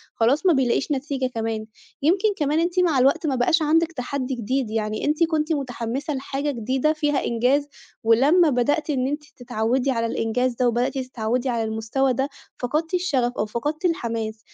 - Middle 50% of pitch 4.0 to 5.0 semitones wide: Yes, average, 4.3 semitones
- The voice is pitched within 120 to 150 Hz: No, very high, 265 Hz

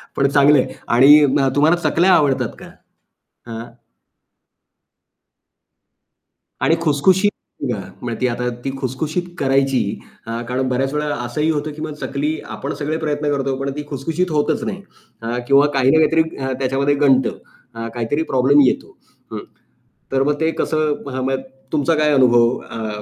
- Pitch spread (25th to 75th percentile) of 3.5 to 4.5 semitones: No, average, 2.8 semitones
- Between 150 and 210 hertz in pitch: No, medium, 140 Hz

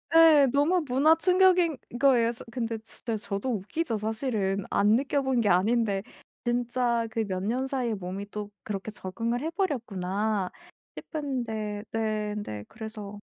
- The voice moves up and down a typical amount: Yes, average, 4.3 semitones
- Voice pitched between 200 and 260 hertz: Yes, high, 225 Hz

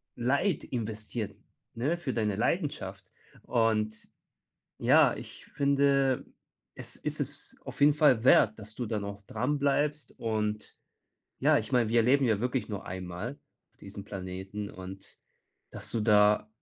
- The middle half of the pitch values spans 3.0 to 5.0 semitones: Yes, average, 4.2 semitones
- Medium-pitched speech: No, low, 110 Hz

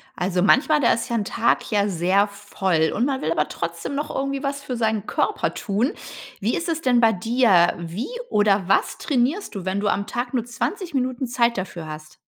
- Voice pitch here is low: No, high, 220 Hz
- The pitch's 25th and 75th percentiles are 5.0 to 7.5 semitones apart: Yes, wide, 5.4 semitones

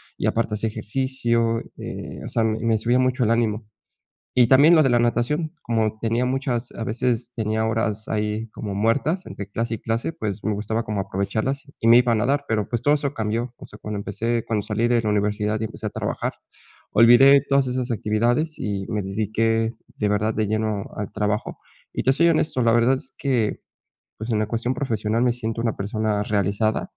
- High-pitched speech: No, low, 115 Hz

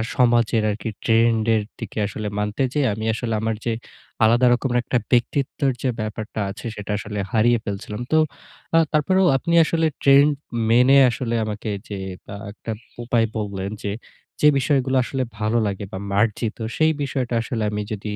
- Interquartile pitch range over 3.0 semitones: Yes, average, 3.6 semitones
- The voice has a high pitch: No, low, 115 Hz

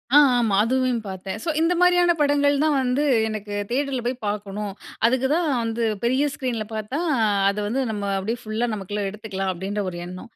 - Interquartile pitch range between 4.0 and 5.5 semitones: Yes, average, 4.5 semitones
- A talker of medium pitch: No, high, 230 Hz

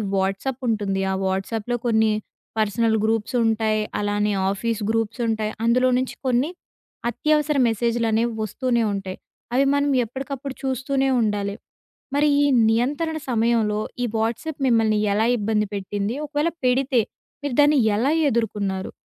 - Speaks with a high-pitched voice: Yes, high, 225 Hz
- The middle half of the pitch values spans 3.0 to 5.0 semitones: Yes, average, 3.6 semitones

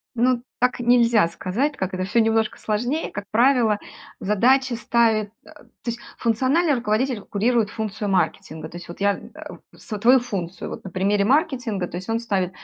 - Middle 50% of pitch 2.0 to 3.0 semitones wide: No, average, 3.7 semitones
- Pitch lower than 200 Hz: No, high, 220 Hz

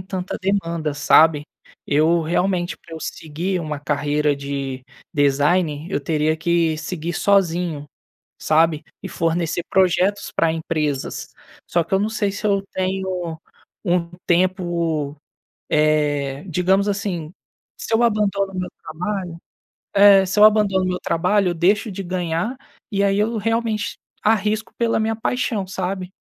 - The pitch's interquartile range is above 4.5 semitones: No, average, 4.0 semitones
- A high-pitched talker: No, medium, 180 Hz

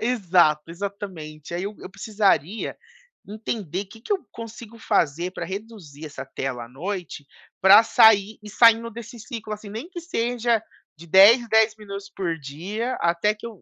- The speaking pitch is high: Yes, high, 205 Hz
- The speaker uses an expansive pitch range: No, average, 4.7 semitones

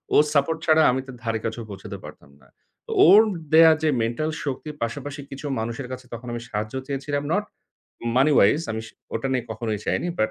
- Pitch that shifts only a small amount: No, average, 4.8 semitones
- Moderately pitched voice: No, low, 130 Hz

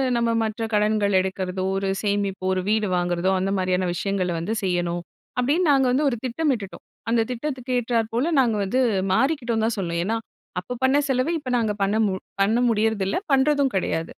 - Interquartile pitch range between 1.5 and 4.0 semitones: No, average, 4.6 semitones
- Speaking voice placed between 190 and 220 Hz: Yes, high, 215 Hz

